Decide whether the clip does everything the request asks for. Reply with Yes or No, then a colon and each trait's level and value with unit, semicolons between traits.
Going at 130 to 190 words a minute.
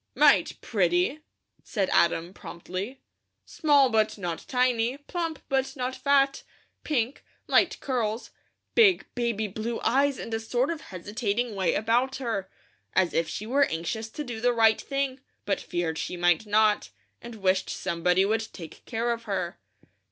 Yes: average, 150 wpm